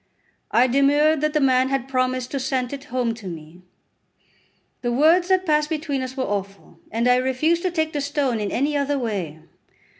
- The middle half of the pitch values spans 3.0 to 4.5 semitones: Yes, average, 3.6 semitones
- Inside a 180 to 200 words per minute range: Yes, average, 190 wpm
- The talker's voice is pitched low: No, very high, 265 Hz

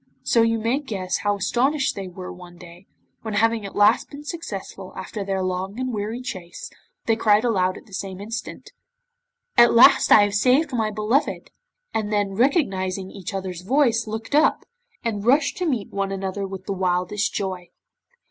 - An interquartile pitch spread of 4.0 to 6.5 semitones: No, average, 3.6 semitones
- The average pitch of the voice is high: Yes, high, 205 Hz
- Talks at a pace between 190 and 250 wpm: No, average, 175 wpm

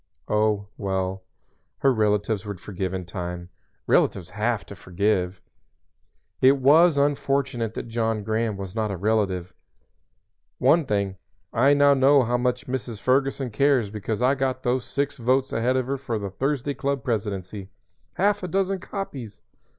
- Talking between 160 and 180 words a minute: No, average, 150 wpm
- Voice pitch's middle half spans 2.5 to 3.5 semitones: No, average, 5.2 semitones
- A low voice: Yes, low, 115 Hz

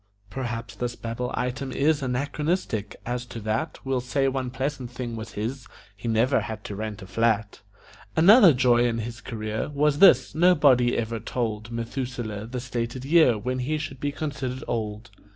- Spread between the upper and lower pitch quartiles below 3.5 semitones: Yes, average, 3.0 semitones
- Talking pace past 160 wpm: Yes, average, 170 wpm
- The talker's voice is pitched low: Yes, low, 125 Hz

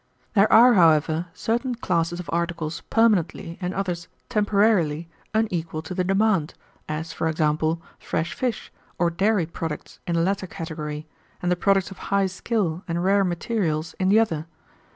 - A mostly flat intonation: No, average, 3.5 semitones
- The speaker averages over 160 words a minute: No, average, 155 wpm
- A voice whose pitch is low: No, medium, 175 Hz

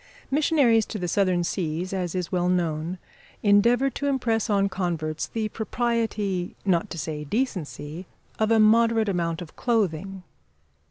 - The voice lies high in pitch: Yes, high, 195 Hz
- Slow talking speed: No, average, 145 wpm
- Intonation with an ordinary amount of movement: Yes, average, 4.4 semitones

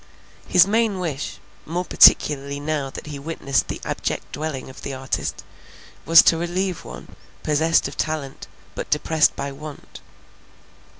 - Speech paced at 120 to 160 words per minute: Yes, average, 140 wpm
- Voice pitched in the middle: Yes, medium, 155 Hz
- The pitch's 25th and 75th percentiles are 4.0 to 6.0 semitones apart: No, average, 3.0 semitones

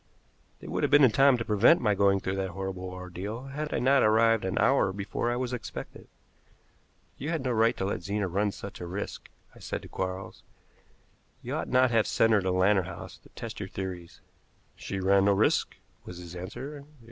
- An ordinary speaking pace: No, fast, 210 wpm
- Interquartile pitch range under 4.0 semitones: No, average, 4.3 semitones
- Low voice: Yes, low, 100 Hz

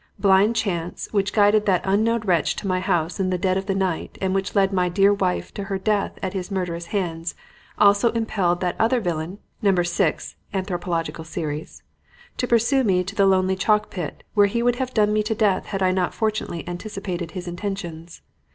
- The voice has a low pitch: No, high, 190 Hz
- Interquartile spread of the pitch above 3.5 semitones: No, average, 2.8 semitones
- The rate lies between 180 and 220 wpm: Yes, average, 195 wpm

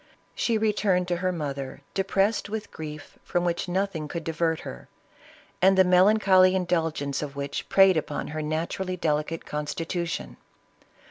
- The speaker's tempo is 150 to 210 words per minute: No, average, 140 wpm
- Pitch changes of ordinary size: Yes, average, 3.7 semitones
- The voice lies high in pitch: No, medium, 170 Hz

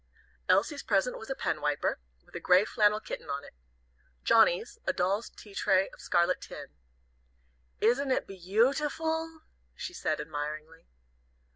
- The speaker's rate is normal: Yes, average, 150 wpm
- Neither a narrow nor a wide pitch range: No, wide, 8.2 semitones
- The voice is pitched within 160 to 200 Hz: No, high, 210 Hz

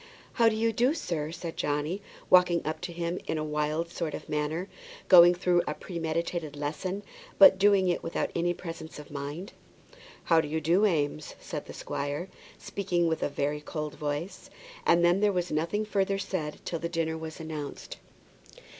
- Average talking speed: Yes, average, 180 wpm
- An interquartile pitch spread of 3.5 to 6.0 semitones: No, average, 3.1 semitones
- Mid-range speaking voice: Yes, medium, 170 Hz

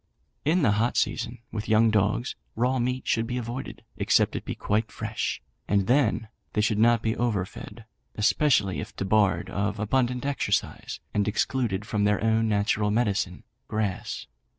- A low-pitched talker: Yes, low, 110 Hz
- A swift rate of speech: No, average, 160 wpm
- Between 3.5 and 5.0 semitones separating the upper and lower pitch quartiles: No, average, 2.7 semitones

